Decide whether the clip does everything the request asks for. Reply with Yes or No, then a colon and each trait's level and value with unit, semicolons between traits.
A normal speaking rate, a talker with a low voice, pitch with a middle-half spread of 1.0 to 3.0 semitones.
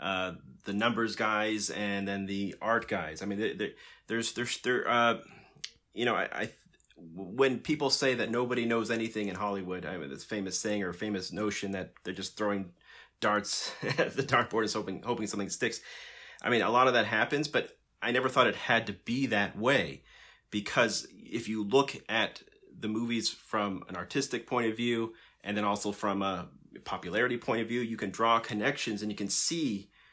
Yes: average, 195 wpm; low, 105 Hz; narrow, 2.6 semitones